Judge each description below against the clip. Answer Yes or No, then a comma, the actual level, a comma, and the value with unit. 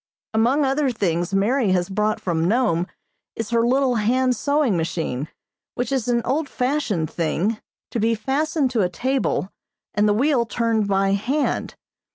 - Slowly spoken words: No, average, 160 wpm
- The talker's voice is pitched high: Yes, high, 230 Hz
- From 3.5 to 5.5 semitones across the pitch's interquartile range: Yes, average, 5.1 semitones